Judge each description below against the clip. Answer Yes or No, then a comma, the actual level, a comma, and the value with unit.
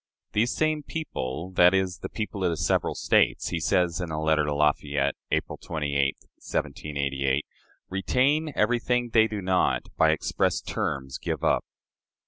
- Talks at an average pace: Yes, average, 150 wpm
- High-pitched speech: No, very low, 90 Hz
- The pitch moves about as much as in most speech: No, wide, 6.9 semitones